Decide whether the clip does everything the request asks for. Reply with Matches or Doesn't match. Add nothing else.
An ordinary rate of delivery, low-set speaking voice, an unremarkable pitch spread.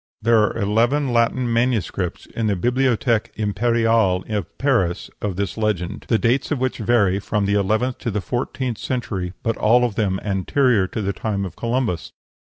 Matches